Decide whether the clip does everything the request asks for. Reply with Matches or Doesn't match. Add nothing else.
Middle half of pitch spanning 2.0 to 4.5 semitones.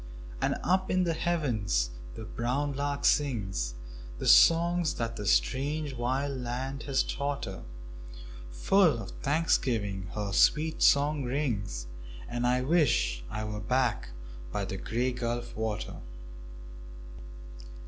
Doesn't match